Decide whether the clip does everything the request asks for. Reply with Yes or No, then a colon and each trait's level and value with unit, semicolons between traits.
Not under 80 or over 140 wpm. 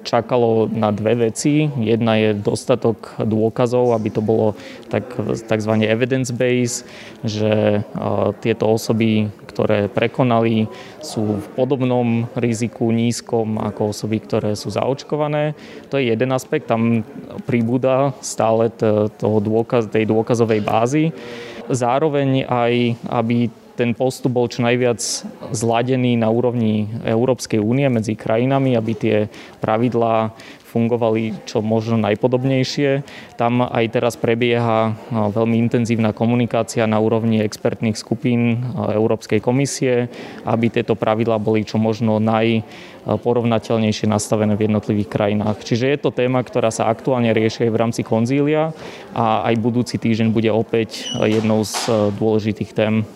Yes: average, 120 wpm